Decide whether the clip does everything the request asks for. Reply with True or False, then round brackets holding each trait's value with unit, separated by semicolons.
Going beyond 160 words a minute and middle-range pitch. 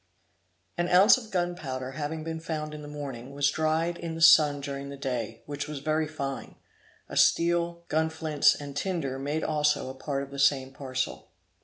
True (180 wpm; 150 Hz)